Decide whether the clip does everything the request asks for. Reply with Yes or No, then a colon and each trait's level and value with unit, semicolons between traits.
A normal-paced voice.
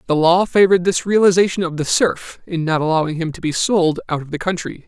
No: fast, 235 wpm